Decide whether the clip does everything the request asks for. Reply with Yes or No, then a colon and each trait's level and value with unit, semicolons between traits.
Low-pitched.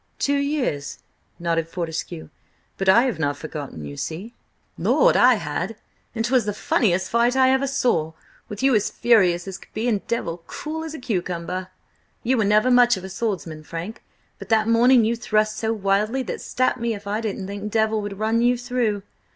No: high, 215 Hz